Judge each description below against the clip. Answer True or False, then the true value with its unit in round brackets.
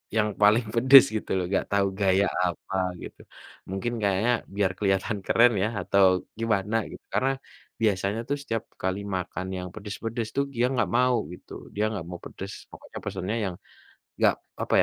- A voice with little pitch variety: False (3.1 semitones)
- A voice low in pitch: True (105 Hz)